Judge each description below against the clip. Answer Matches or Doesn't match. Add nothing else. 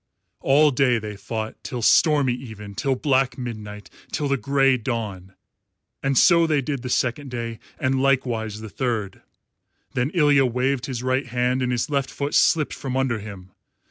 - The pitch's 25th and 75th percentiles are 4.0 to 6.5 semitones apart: Doesn't match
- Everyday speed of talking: Matches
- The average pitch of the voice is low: Matches